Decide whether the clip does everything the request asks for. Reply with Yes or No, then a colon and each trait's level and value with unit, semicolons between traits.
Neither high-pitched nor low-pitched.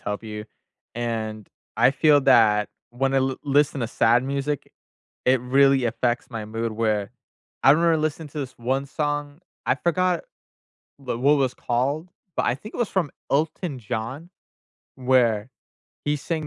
No: low, 130 Hz